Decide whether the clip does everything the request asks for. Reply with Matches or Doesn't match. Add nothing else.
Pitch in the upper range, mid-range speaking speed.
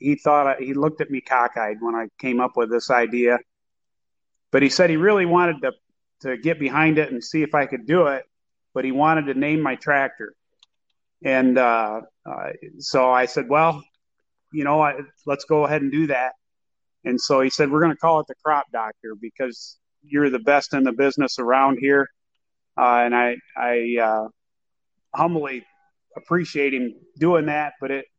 Doesn't match